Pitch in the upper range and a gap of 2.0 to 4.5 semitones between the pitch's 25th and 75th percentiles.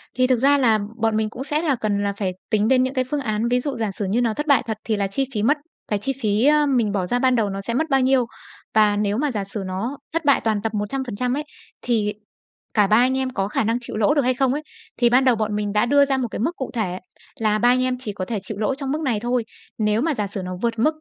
Yes: high, 235 Hz; average, 3.9 semitones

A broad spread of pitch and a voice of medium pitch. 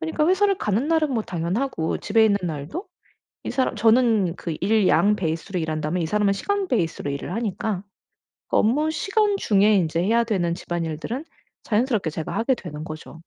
No: wide, 6.7 semitones; high, 205 Hz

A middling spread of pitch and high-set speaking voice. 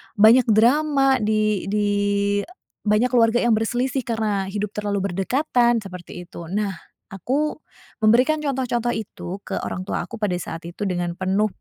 Yes: average, 3.7 semitones; high, 215 Hz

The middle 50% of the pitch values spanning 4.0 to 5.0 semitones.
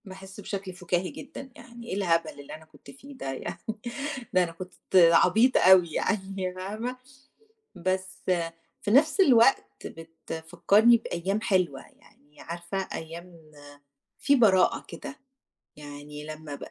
Yes: average, 4.4 semitones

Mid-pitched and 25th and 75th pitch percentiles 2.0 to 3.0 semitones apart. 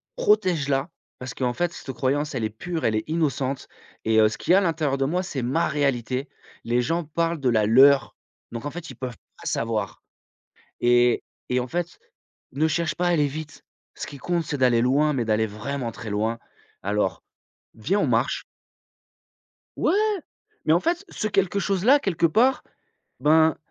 No: medium, 145 Hz; wide, 5.5 semitones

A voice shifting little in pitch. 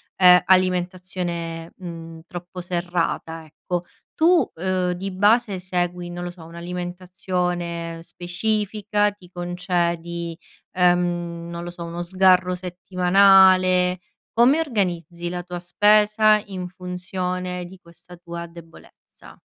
Yes: narrow, 1.4 semitones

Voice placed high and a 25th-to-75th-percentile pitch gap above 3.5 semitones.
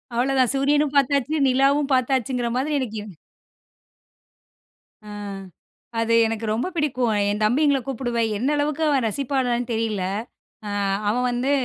No: very high, 255 Hz; average, 3.2 semitones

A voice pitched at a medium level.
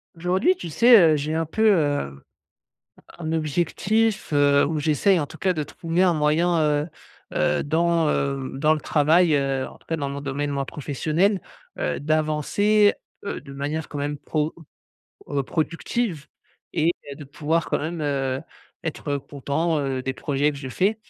Yes: medium, 155 Hz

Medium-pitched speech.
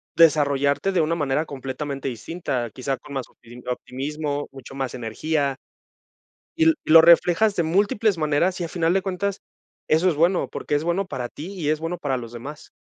Yes: medium, 155 Hz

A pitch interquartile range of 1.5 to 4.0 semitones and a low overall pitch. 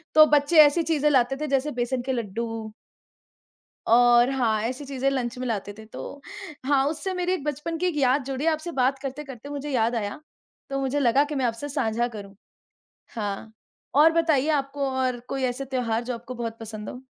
No: average, 3.5 semitones; very high, 265 Hz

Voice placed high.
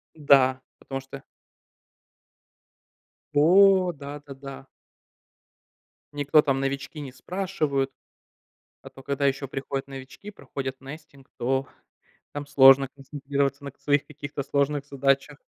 No: medium, 140 Hz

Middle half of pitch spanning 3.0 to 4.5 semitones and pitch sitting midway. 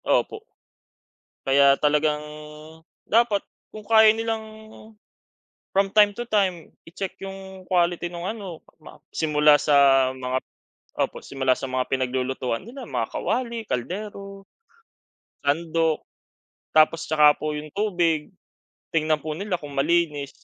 No: average, 5.2 semitones; medium, 165 Hz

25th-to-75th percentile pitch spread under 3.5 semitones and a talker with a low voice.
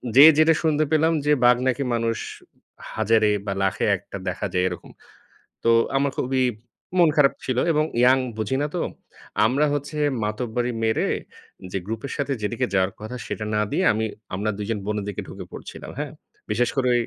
No: average, 4.6 semitones; low, 120 Hz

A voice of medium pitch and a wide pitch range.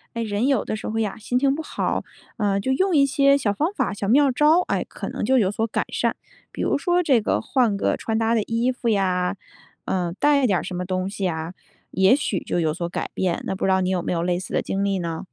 No: high, 210 Hz; wide, 5.9 semitones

